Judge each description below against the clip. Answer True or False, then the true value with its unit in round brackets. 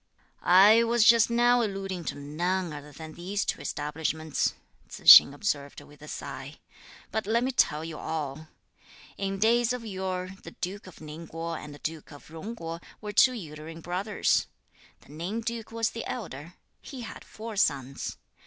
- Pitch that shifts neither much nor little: False (6.0 semitones)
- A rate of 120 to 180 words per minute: True (170 wpm)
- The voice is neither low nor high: True (180 Hz)